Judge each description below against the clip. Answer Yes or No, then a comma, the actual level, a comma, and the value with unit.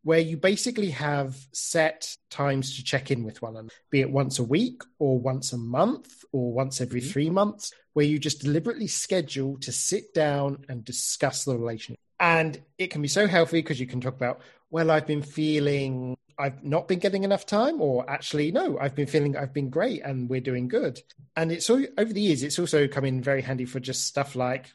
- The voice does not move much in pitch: No, average, 3.8 semitones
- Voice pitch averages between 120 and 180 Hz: Yes, medium, 140 Hz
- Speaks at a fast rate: Yes, fast, 215 wpm